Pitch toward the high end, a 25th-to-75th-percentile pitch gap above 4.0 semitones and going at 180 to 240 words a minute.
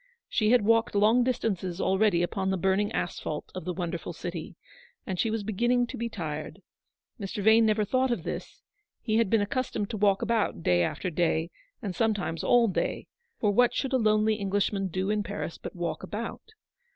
No: high, 205 Hz; average, 3.7 semitones; average, 190 wpm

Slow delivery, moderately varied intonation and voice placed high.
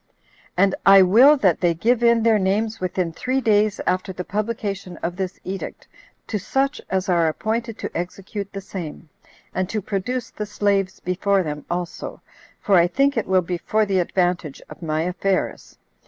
No: average, 175 wpm; average, 3.2 semitones; high, 195 Hz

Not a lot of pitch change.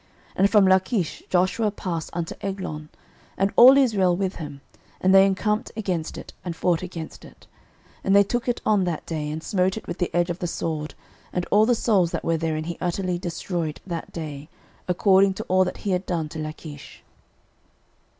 No: average, 3.0 semitones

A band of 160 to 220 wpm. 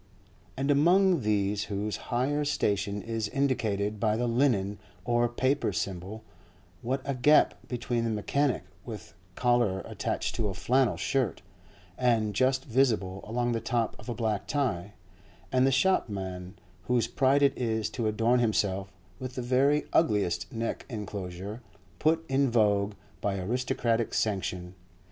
No: average, 140 wpm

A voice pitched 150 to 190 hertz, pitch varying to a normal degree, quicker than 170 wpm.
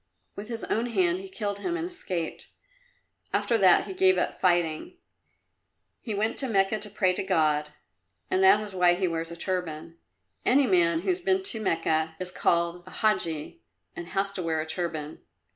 Yes: medium, 185 Hz; average, 4.2 semitones; average, 180 wpm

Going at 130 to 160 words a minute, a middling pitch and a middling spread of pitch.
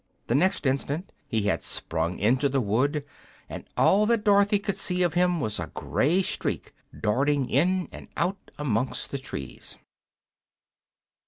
No: average, 150 wpm; medium, 145 Hz; wide, 6.9 semitones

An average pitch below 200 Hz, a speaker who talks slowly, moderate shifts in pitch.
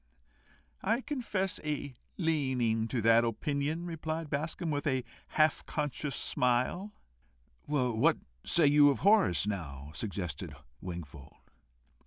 No: medium, 140 Hz; slow, 115 wpm; wide, 6.3 semitones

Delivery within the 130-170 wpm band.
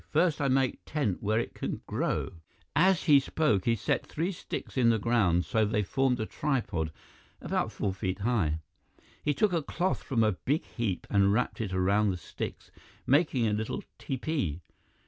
No: average, 185 wpm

